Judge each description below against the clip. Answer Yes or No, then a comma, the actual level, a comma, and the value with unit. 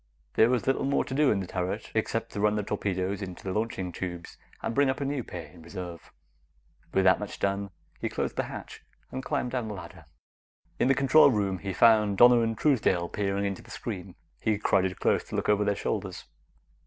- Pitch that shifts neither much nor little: Yes, average, 4.4 semitones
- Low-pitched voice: Yes, low, 100 Hz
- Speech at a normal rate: No, fast, 215 wpm